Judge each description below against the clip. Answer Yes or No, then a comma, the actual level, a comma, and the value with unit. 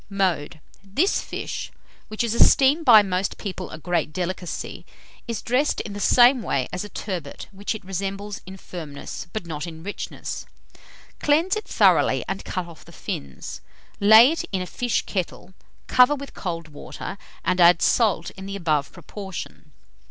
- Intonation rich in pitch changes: No, average, 4.1 semitones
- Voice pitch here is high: Yes, high, 195 Hz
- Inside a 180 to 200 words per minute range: No, average, 165 wpm